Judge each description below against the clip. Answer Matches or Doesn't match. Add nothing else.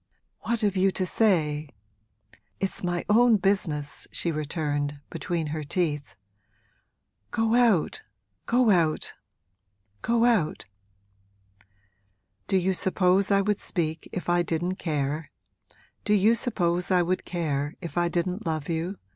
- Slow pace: Matches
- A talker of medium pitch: Matches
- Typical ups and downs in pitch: Matches